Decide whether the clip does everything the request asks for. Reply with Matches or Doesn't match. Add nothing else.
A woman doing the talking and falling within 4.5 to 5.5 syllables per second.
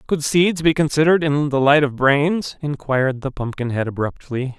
Doesn't match